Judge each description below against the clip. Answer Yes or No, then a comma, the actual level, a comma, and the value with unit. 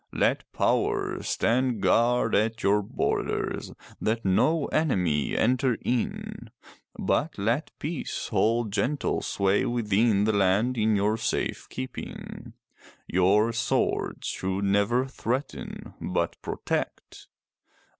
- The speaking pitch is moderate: No, low, 110 Hz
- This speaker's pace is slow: Yes, slow, 105 wpm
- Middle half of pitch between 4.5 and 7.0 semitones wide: No, average, 3.8 semitones